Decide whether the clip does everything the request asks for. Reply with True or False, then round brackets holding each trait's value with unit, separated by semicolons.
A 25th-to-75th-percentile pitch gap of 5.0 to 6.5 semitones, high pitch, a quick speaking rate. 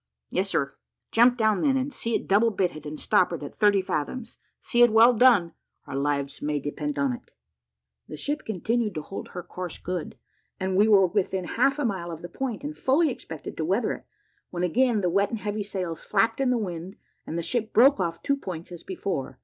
True (5.5 semitones; 195 Hz; 215 wpm)